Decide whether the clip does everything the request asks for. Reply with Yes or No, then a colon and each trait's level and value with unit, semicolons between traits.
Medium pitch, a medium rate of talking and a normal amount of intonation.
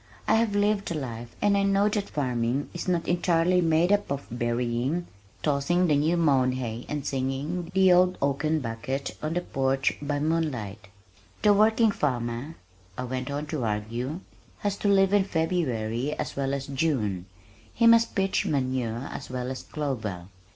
No: medium, 145 Hz; average, 170 wpm; wide, 5.9 semitones